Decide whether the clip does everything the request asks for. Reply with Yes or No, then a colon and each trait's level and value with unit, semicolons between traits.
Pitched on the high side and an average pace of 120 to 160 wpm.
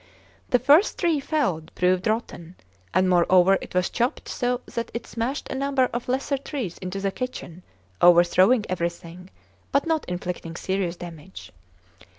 Yes: high, 195 Hz; average, 150 wpm